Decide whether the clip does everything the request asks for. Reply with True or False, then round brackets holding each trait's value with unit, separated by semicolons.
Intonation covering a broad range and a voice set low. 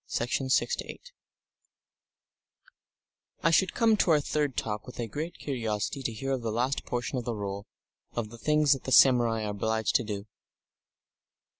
False (3.9 semitones; 120 Hz)